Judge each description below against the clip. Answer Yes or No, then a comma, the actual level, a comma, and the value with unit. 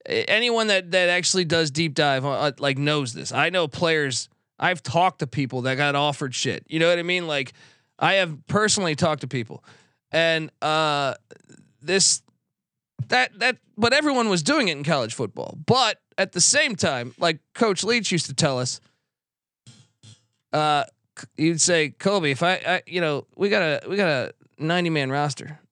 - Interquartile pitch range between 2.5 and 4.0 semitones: No, average, 4.4 semitones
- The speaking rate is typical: Yes, average, 180 wpm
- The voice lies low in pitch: No, medium, 155 Hz